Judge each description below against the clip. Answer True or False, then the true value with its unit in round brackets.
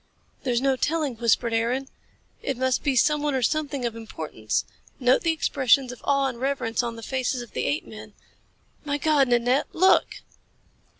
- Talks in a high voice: True (260 Hz)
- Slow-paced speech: False (165 wpm)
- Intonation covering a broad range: False (3.1 semitones)